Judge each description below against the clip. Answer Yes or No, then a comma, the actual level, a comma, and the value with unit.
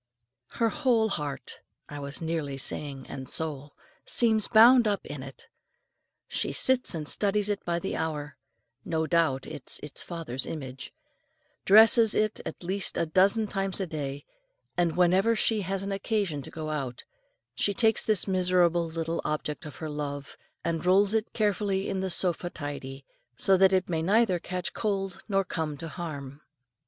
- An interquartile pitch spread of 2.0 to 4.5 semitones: No, average, 5.2 semitones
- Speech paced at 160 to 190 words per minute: Yes, average, 165 wpm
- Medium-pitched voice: Yes, medium, 175 Hz